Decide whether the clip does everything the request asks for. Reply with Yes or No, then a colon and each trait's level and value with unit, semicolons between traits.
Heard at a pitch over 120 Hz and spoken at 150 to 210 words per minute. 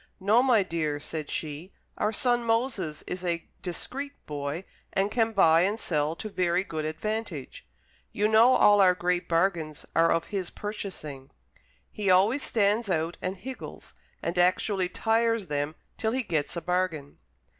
Yes: medium, 185 Hz; average, 155 wpm